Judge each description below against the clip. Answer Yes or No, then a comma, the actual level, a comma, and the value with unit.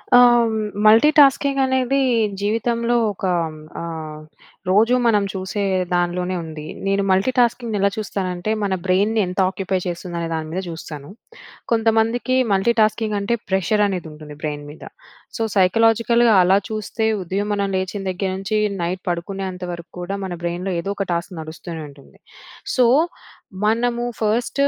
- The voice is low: No, high, 195 Hz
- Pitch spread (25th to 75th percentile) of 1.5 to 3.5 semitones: No, average, 4.2 semitones